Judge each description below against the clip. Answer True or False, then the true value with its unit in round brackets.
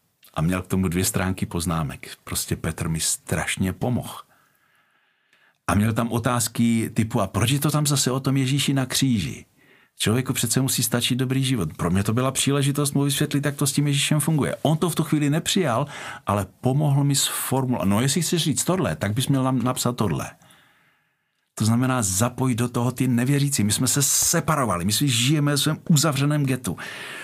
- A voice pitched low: True (130 Hz)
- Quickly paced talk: True (190 wpm)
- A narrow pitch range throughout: False (4.5 semitones)